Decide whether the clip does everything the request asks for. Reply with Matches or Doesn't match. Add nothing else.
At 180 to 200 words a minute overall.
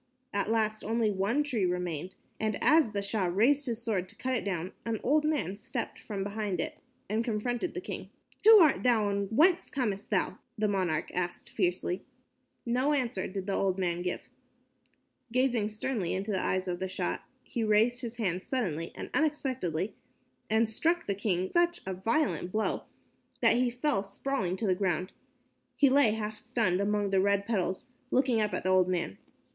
Matches